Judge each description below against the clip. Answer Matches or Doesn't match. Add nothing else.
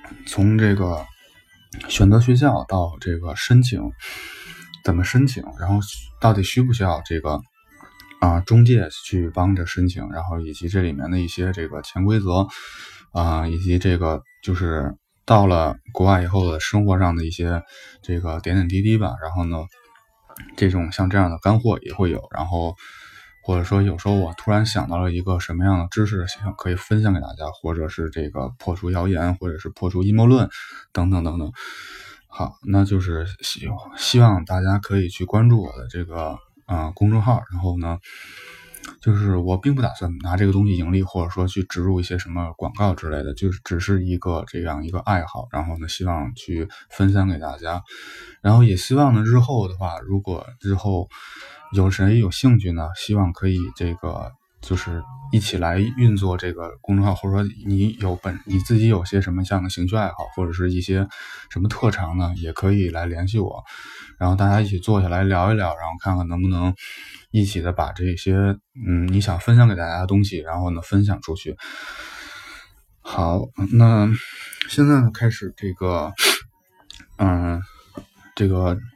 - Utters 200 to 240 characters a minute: Doesn't match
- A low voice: Matches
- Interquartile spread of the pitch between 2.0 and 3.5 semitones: Matches